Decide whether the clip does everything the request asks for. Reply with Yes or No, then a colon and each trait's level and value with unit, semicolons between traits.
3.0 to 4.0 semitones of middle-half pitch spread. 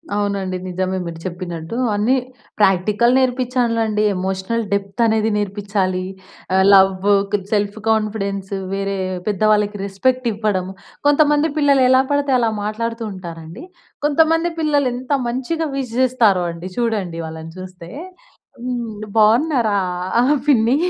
No: average, 4.6 semitones